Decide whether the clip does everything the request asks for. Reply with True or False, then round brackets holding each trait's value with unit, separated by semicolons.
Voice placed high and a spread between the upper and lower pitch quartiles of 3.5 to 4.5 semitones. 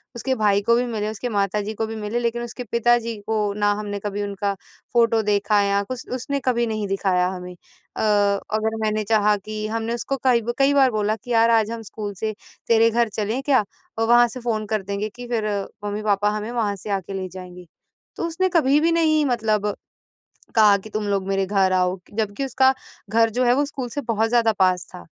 False (220 Hz; 2.7 semitones)